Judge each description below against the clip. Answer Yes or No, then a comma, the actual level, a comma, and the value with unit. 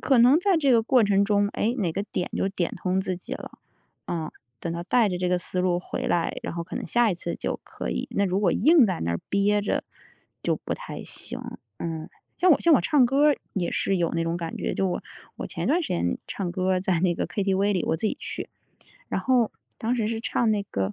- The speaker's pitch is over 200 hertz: No, high, 195 Hz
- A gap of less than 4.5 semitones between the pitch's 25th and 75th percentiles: No, average, 4.9 semitones